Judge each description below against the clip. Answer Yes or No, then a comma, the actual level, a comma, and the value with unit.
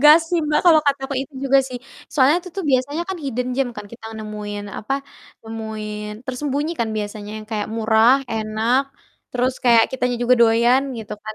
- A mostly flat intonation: No, average, 3.9 semitones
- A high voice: Yes, high, 245 Hz